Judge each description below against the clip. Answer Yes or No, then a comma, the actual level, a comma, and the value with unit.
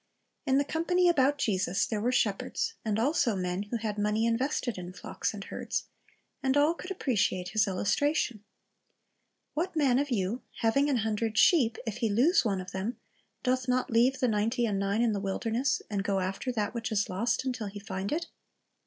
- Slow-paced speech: No, average, 190 wpm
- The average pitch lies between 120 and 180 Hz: No, high, 225 Hz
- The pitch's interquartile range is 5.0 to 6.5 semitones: No, average, 4.4 semitones